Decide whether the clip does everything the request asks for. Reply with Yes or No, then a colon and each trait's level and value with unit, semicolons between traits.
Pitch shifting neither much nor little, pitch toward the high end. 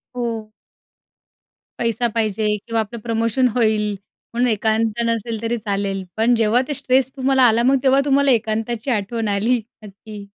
No: narrow, 2.3 semitones; high, 230 Hz